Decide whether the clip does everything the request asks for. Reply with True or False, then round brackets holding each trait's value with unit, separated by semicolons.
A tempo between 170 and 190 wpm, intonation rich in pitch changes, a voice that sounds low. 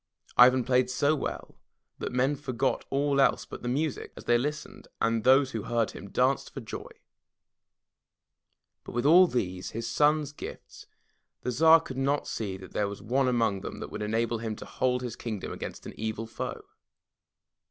False (180 wpm; 3.5 semitones; 125 Hz)